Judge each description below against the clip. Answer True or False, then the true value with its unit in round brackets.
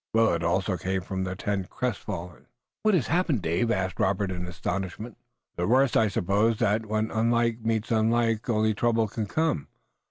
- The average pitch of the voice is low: True (110 Hz)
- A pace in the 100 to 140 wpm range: False (165 wpm)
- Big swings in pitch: False (3.5 semitones)